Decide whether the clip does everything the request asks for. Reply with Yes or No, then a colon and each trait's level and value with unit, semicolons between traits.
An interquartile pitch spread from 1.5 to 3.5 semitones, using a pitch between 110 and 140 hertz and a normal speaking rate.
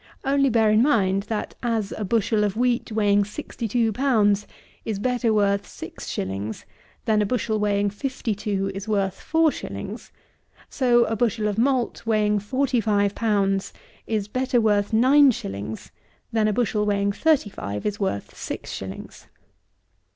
No: average, 2.9 semitones; high, 215 Hz; average, 160 wpm